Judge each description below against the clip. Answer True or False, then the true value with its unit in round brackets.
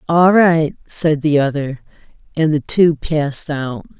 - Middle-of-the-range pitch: True (155 Hz)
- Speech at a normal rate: True (150 wpm)